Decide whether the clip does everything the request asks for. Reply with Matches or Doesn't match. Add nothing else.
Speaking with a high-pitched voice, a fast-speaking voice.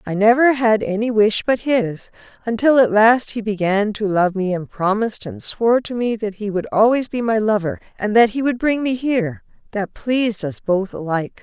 Matches